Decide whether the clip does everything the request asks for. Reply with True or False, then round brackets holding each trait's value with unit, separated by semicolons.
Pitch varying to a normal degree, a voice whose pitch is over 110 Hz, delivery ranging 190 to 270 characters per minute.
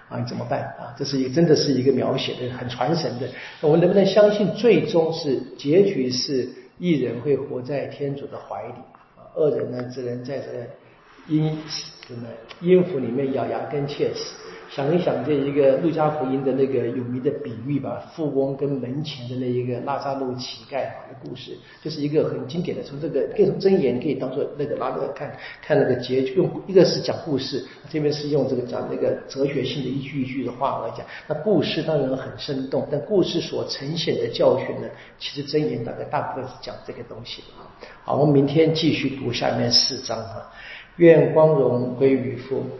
False (3.4 semitones; 140 Hz; 295 characters per minute)